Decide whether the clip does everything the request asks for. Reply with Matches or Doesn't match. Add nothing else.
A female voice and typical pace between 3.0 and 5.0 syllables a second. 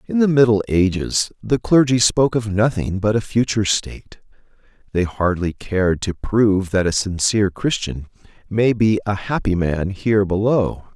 Doesn't match